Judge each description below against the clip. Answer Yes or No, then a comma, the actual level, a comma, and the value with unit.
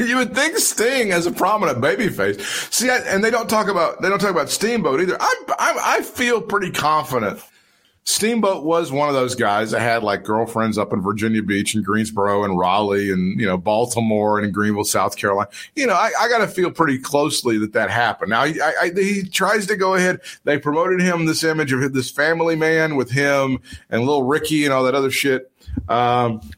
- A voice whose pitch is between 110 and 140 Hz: Yes, low, 135 Hz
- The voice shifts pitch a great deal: Yes, wide, 8.8 semitones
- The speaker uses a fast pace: Yes, fast, 210 wpm